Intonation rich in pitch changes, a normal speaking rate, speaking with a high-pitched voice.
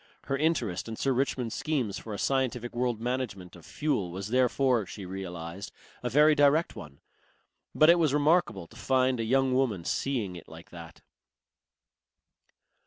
No: wide, 6.0 semitones; average, 160 wpm; low, 120 Hz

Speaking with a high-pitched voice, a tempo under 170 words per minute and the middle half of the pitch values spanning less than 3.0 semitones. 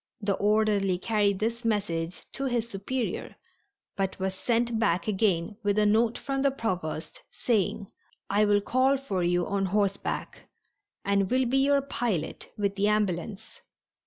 No: high, 210 Hz; average, 150 wpm; average, 3.3 semitones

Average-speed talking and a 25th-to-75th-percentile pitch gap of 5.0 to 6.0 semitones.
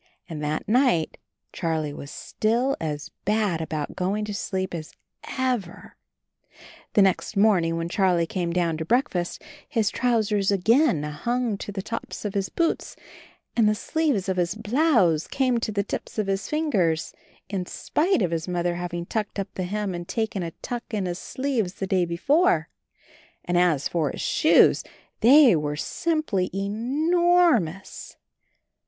Yes: average, 160 wpm; wide, 5.4 semitones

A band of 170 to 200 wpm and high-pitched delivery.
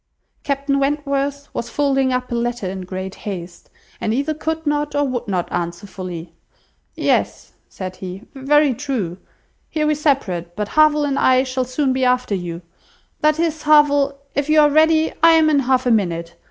Yes: average, 180 wpm; very high, 265 Hz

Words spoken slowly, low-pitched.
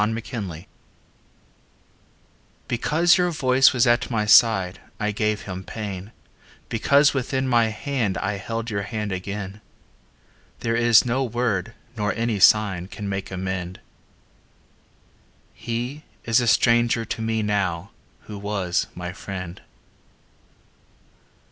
Yes: slow, 115 wpm; low, 110 Hz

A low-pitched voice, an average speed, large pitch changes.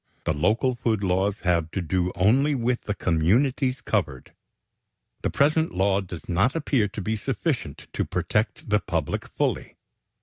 Yes: low, 105 Hz; average, 155 wpm; wide, 5.8 semitones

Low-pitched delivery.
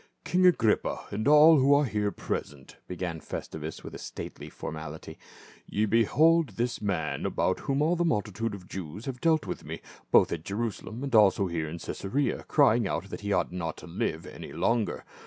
Yes: low, 105 Hz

